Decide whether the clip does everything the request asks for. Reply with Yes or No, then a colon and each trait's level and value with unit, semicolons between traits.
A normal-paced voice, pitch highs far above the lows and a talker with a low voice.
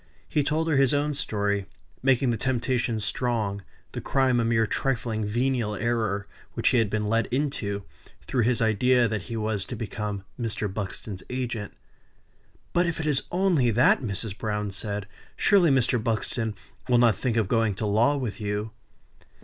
No: average, 170 wpm; average, 3.5 semitones; low, 115 Hz